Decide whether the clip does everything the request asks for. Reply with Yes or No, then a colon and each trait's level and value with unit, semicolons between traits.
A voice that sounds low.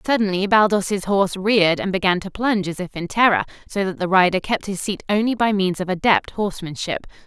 No: high, 195 Hz